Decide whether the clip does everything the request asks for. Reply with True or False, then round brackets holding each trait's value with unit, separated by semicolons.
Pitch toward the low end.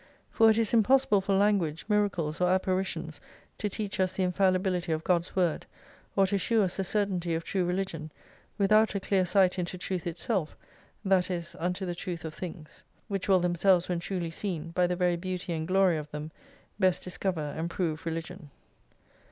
False (180 Hz)